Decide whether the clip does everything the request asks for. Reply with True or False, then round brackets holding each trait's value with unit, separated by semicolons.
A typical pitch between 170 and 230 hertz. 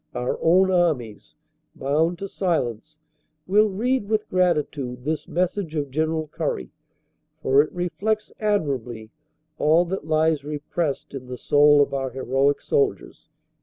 False (155 Hz)